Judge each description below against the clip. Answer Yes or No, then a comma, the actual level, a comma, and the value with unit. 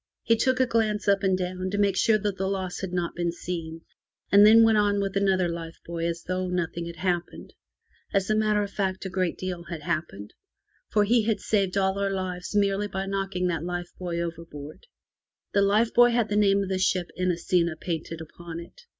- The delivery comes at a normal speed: No, fast, 215 wpm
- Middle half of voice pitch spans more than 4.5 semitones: No, average, 2.9 semitones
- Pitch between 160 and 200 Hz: Yes, high, 190 Hz